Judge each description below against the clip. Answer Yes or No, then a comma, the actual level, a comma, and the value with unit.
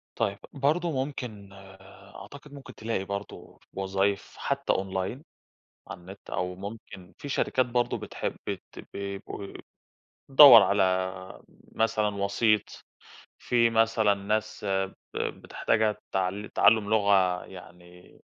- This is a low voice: Yes, low, 100 Hz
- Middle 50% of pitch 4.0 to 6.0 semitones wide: No, average, 3.2 semitones